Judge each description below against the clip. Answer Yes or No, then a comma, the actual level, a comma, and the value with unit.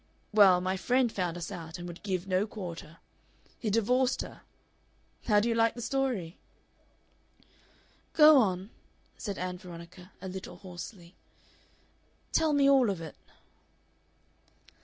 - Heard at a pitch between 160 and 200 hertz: Yes, high, 190 Hz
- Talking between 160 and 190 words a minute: No, slow, 135 wpm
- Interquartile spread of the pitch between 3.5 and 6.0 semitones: Yes, average, 4.6 semitones